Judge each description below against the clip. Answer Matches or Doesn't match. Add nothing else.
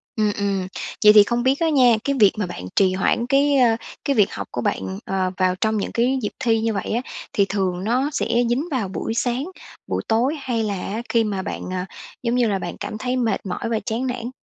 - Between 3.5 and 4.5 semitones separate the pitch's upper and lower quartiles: Matches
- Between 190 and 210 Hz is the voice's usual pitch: Doesn't match